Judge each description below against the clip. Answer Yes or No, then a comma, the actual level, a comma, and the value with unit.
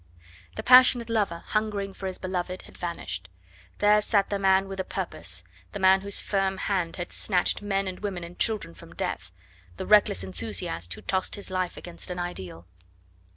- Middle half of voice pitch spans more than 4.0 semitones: No, narrow, 2.4 semitones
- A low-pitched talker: No, high, 190 Hz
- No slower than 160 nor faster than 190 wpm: Yes, average, 180 wpm